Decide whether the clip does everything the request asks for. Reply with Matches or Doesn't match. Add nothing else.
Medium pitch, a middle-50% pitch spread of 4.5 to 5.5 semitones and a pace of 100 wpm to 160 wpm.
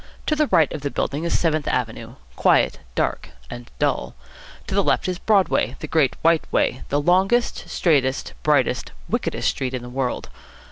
Doesn't match